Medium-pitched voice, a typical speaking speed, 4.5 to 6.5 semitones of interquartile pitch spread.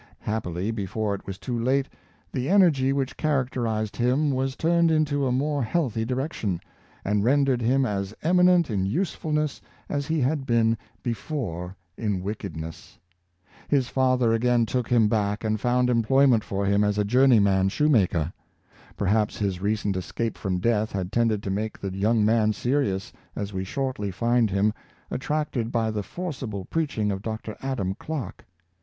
No: low, 115 Hz; average, 160 wpm; average, 4.9 semitones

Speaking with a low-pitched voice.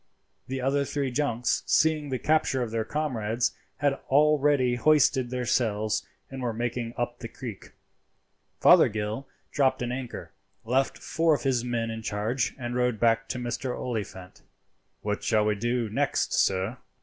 Yes: low, 125 Hz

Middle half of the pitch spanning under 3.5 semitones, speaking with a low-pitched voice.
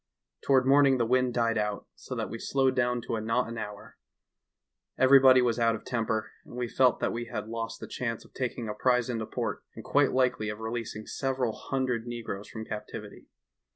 Yes: narrow, 2.4 semitones; low, 120 Hz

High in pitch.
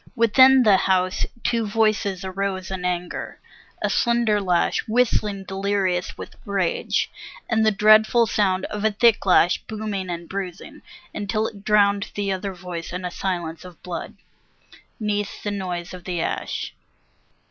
Yes: high, 200 Hz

